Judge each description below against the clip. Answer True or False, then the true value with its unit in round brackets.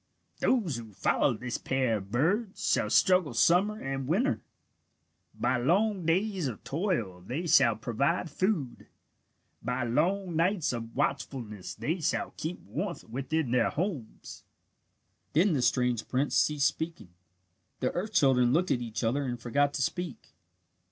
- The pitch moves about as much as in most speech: False (6.7 semitones)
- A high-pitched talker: False (140 Hz)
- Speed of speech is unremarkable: True (145 wpm)